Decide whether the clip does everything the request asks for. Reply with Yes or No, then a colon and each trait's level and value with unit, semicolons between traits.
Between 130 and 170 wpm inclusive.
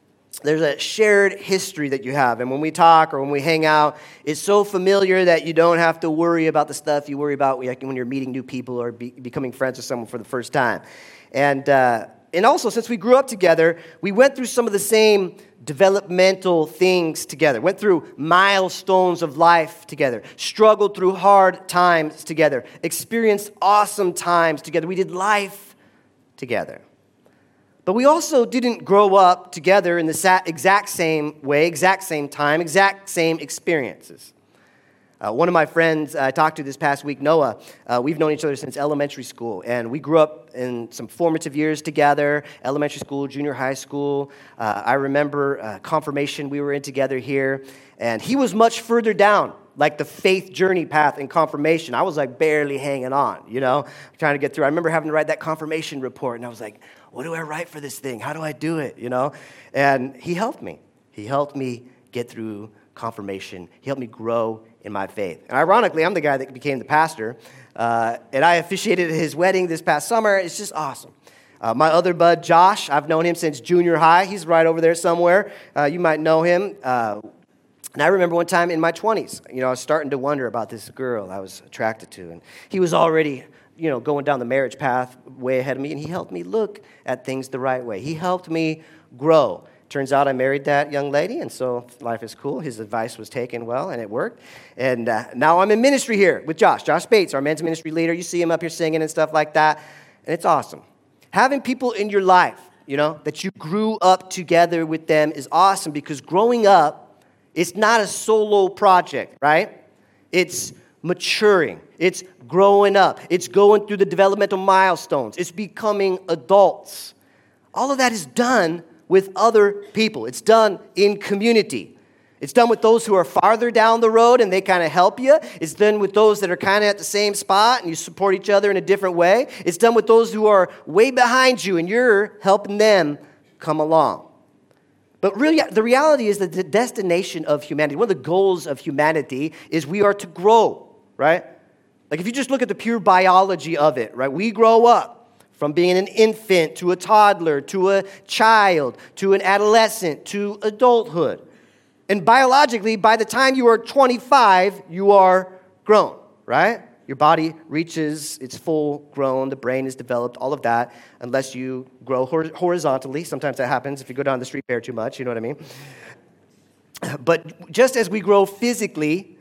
No: average, 200 wpm